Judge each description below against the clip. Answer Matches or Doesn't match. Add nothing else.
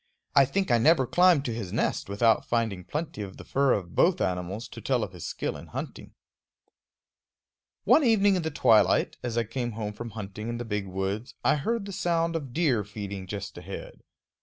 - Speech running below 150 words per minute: Doesn't match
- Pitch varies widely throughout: Matches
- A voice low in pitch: Matches